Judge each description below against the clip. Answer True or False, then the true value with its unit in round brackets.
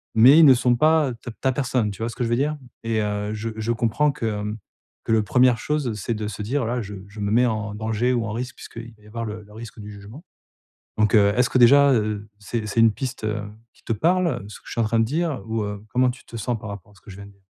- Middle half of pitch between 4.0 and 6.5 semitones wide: False (2.9 semitones)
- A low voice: True (115 Hz)